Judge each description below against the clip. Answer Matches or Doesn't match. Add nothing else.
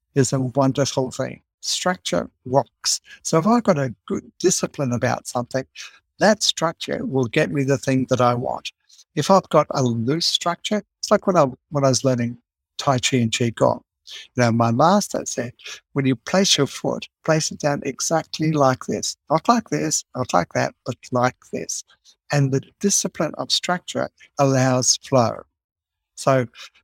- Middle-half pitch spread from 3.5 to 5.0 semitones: Matches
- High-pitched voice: Doesn't match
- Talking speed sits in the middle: Matches